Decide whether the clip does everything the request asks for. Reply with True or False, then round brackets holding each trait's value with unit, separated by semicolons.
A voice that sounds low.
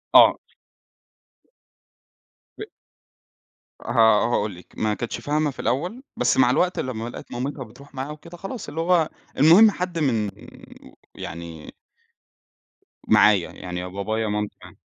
True (130 Hz)